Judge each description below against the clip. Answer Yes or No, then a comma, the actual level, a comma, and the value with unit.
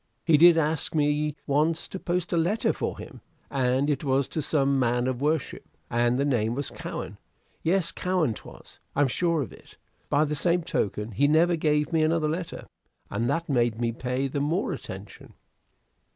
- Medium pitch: Yes, medium, 150 Hz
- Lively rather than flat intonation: No, average, 4.0 semitones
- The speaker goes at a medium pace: Yes, average, 180 wpm